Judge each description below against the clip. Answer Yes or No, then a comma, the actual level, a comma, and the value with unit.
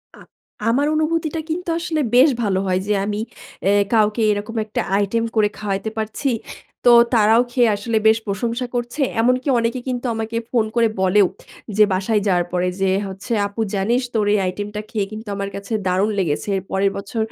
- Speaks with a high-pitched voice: Yes, high, 215 Hz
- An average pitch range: Yes, average, 3.2 semitones